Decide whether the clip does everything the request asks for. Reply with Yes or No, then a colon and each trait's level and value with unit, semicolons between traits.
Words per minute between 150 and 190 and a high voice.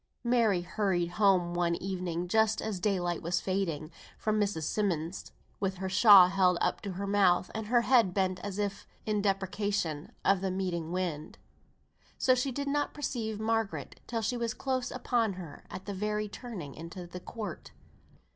Yes: average, 170 wpm; high, 195 Hz